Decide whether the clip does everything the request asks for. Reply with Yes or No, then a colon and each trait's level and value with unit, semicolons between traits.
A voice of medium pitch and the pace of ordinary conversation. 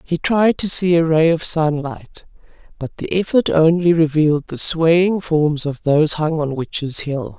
Yes: medium, 160 Hz; average, 180 wpm